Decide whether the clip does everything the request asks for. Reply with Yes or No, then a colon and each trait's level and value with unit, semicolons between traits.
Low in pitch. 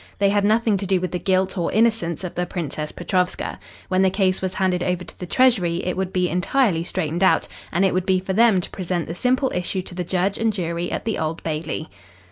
No: medium, 185 Hz